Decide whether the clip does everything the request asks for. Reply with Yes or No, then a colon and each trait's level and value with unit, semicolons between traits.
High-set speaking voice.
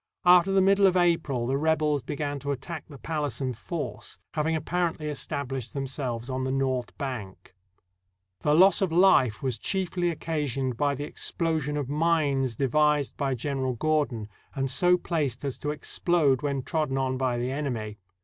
No: medium, 145 Hz